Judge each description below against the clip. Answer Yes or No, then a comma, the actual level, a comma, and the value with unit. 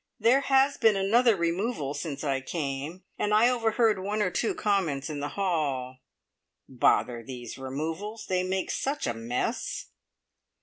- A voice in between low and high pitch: Yes, medium, 180 Hz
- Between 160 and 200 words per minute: No, average, 145 wpm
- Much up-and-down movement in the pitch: Yes, wide, 7.7 semitones